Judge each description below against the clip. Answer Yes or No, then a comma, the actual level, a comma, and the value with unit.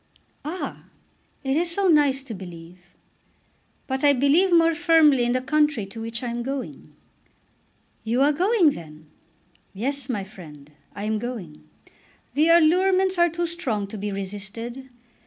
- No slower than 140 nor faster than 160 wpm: Yes, average, 150 wpm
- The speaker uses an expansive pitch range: Yes, wide, 7.8 semitones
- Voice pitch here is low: No, very high, 265 Hz